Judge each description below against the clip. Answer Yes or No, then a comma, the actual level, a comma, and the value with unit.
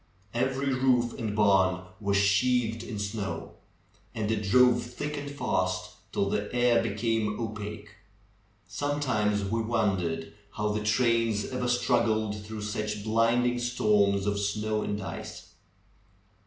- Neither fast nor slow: No, slow, 130 wpm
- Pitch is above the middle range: No, low, 110 Hz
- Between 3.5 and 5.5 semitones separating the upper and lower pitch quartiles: No, average, 2.9 semitones